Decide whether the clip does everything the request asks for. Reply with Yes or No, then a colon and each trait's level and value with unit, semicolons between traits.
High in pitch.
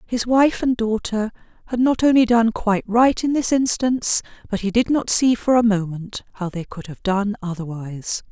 Yes: high, 220 Hz